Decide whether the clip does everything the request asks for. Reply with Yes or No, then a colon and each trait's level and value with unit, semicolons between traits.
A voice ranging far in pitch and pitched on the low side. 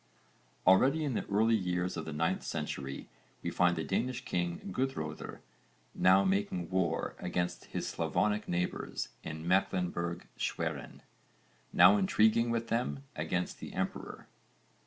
No: average, 3.6 semitones; very low, 90 Hz